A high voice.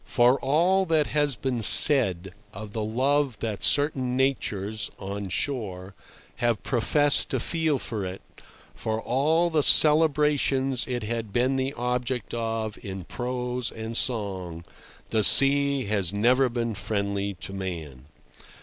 No: low, 120 Hz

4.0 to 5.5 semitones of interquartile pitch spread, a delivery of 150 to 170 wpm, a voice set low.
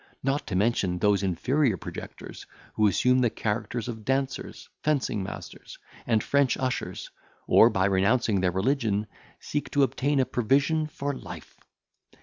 No: average, 5.1 semitones; average, 140 wpm; low, 120 Hz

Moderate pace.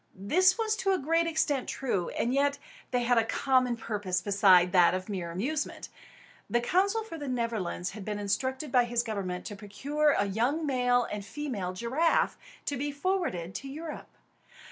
Yes: average, 175 wpm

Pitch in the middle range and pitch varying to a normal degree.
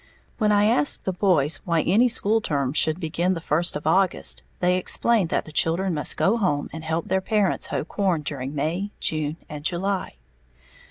Yes: medium, 175 Hz; average, 4.0 semitones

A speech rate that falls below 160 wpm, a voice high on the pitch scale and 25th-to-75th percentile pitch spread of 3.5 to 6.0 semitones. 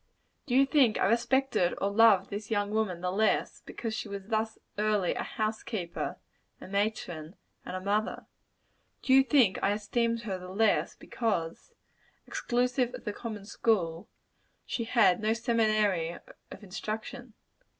No: average, 150 wpm; high, 215 Hz; average, 3.0 semitones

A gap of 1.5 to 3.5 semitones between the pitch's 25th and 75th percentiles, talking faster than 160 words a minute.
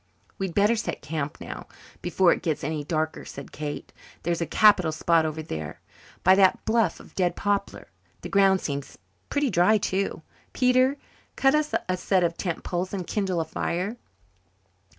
No: average, 4.2 semitones; average, 170 wpm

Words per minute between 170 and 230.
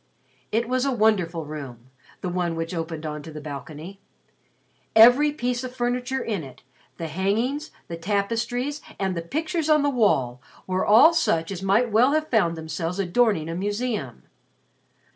No: average, 160 wpm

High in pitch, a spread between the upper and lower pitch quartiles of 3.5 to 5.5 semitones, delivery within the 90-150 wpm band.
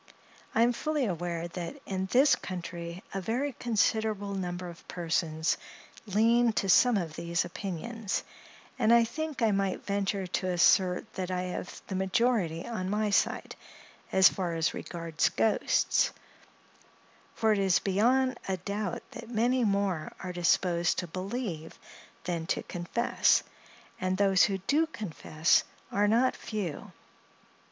Yes: high, 195 Hz; average, 4.2 semitones; slow, 135 wpm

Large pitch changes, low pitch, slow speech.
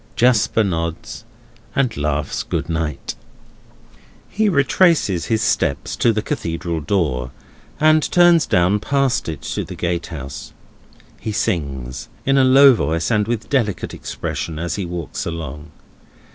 Yes: wide, 7.8 semitones; very low, 90 Hz; slow, 130 wpm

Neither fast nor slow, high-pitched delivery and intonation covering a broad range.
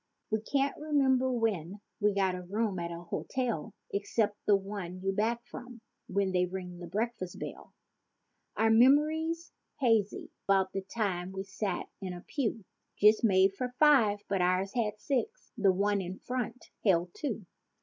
No: average, 160 wpm; high, 205 Hz; average, 4.2 semitones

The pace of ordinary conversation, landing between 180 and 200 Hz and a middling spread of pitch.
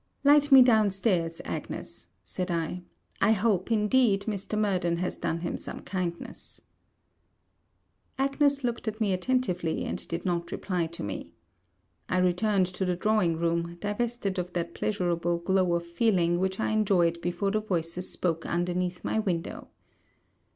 Yes: average, 150 wpm; medium, 185 Hz; average, 3.8 semitones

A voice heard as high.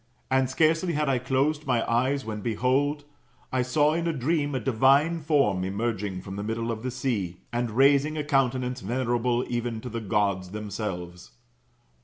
No: low, 125 Hz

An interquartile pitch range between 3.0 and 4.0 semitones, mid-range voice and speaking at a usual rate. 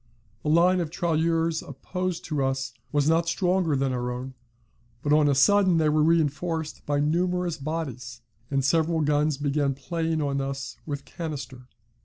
Yes: average, 3.3 semitones; medium, 150 Hz; average, 160 wpm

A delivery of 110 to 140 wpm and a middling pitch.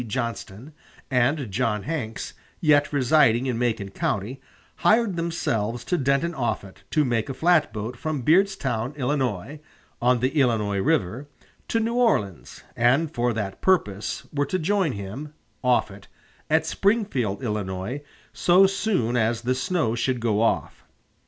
No: slow, 135 wpm; low, 125 Hz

